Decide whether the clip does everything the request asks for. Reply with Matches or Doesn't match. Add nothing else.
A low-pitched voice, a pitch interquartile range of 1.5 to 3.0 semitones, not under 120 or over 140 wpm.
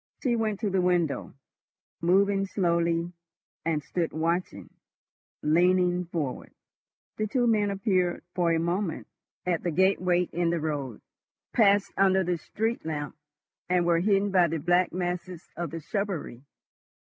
Doesn't match